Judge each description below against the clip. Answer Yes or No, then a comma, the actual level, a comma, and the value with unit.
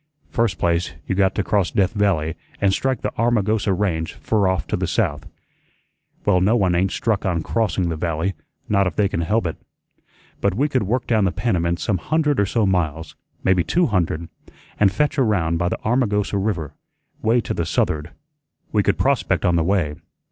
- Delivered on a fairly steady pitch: No, average, 4.2 semitones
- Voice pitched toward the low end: Yes, very low, 95 Hz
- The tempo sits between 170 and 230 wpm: Yes, average, 190 wpm